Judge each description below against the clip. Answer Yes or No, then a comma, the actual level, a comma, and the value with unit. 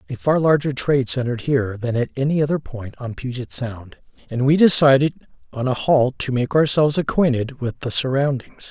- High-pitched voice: No, low, 135 Hz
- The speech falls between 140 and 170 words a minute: No, average, 185 wpm